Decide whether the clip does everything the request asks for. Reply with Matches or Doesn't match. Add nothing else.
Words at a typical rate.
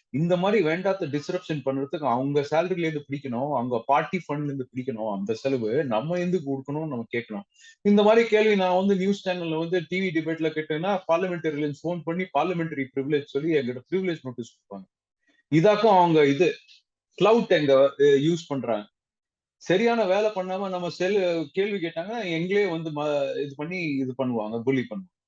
Doesn't match